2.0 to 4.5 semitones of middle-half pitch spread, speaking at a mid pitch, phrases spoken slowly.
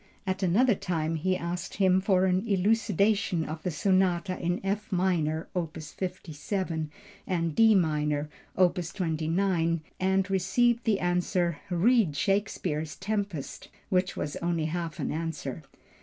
Yes: average, 3.0 semitones; medium, 180 Hz; slow, 130 wpm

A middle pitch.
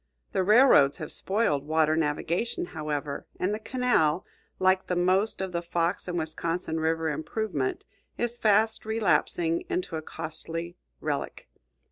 Yes: medium, 170 Hz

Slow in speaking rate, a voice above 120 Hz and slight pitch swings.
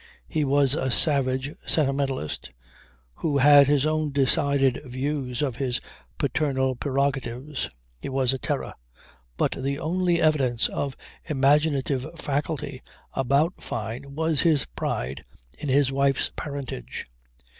Yes: slow, 120 wpm; medium, 140 Hz; narrow, 2.0 semitones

